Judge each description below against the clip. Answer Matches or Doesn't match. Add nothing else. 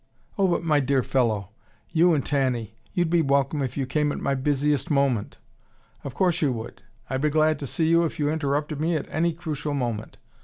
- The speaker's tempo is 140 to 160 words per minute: Doesn't match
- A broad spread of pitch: Doesn't match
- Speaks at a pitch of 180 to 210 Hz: Doesn't match